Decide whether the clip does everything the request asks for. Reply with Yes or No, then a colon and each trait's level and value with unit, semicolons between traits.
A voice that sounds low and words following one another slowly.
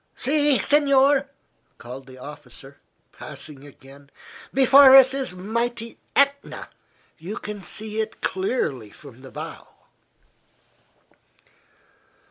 No: high, 210 Hz; slow, 100 wpm